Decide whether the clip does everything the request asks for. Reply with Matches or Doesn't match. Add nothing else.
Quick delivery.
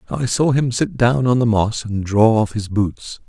Matches